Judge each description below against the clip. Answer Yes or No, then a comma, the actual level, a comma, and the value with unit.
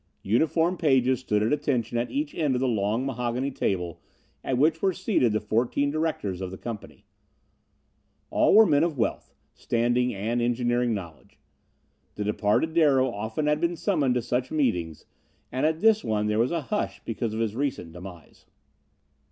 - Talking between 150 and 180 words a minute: Yes, average, 170 wpm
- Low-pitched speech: Yes, low, 125 Hz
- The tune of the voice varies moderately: No, wide, 5.7 semitones